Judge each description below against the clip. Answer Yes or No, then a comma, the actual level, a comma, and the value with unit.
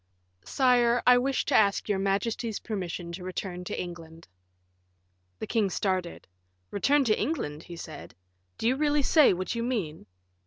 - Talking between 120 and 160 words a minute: Yes, average, 155 wpm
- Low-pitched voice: No, high, 200 Hz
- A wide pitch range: Yes, wide, 5.7 semitones